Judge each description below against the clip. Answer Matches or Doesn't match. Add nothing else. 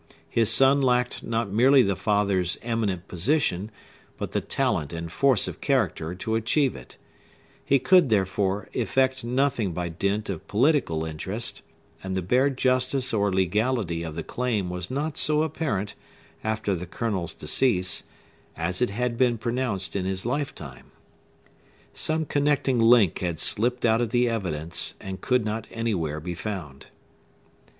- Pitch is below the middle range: Matches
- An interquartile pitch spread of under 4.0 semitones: Doesn't match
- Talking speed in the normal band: Matches